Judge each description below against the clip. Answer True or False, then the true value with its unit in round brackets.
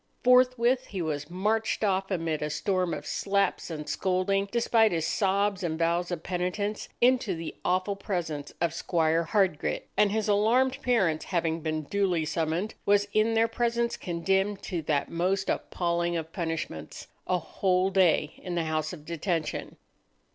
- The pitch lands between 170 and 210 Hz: True (185 Hz)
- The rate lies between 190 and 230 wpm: False (155 wpm)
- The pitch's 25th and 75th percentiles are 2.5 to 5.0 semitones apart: True (3.8 semitones)